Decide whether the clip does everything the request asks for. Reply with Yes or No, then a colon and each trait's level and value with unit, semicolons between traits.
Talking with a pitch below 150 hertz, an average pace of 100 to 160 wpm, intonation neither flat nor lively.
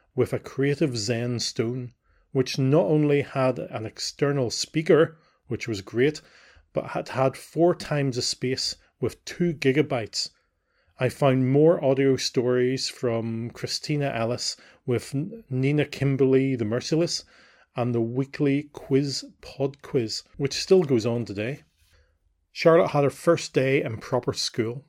Yes: low, 135 Hz; slow, 135 wpm; average, 3.4 semitones